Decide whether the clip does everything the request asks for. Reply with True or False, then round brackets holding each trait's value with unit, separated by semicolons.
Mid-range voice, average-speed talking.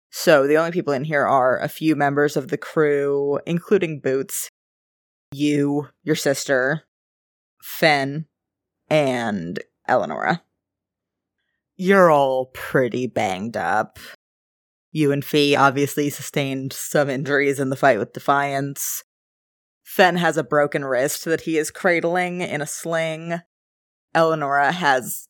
False (145 Hz; 125 wpm)